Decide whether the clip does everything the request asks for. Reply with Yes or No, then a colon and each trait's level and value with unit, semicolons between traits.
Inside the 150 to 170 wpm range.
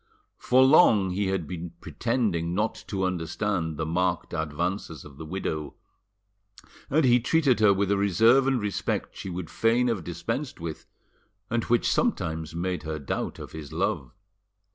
Yes: average, 160 wpm